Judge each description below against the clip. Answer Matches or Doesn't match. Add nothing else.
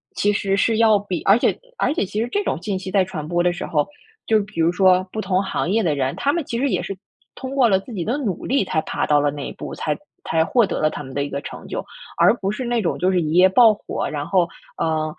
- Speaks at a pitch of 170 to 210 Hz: Matches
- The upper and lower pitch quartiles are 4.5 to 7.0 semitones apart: Matches